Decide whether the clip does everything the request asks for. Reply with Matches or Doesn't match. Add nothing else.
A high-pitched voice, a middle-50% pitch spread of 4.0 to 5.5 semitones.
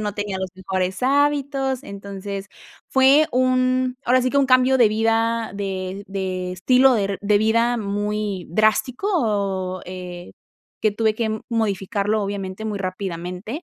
Matches